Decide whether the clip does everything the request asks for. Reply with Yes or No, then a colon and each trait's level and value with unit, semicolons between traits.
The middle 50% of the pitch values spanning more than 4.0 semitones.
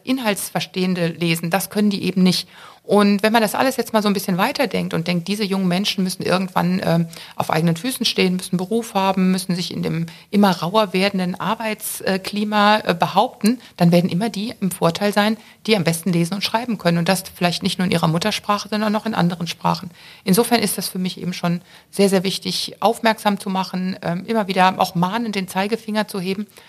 No: average, 2.9 semitones